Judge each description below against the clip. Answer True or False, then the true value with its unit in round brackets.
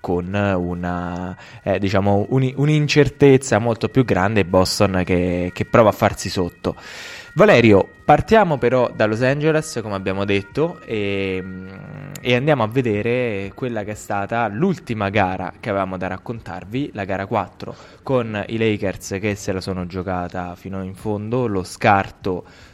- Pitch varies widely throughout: False (4.6 semitones)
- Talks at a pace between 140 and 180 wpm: True (145 wpm)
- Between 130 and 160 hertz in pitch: False (100 Hz)